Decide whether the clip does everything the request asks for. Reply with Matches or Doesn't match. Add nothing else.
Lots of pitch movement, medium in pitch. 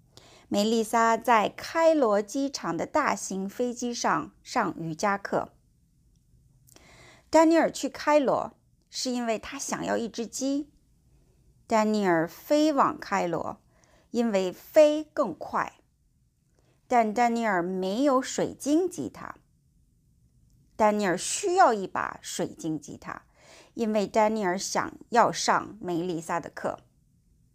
Doesn't match